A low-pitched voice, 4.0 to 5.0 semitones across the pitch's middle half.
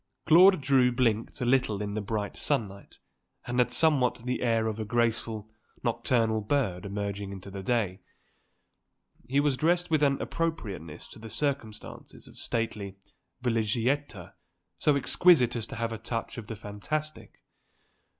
Yes: low, 115 Hz; average, 4.5 semitones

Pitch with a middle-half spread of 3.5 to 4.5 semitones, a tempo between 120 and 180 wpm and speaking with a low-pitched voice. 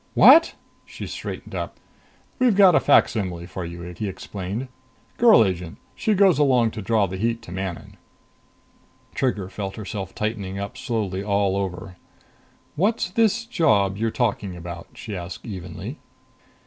No: average, 5.2 semitones; average, 145 wpm; low, 100 Hz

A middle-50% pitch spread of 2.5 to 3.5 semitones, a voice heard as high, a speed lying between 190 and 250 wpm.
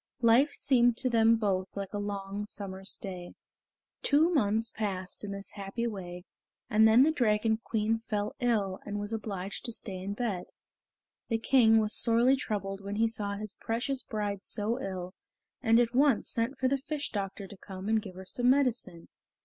No: average, 3.1 semitones; high, 215 Hz; average, 180 wpm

